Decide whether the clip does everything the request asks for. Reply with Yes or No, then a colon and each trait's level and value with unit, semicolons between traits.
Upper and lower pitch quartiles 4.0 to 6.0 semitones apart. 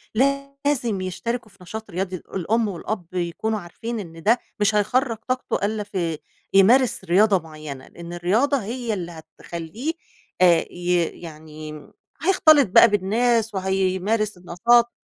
Yes: average, 5.0 semitones